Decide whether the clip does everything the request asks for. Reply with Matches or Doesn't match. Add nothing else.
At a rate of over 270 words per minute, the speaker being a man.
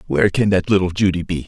Doesn't match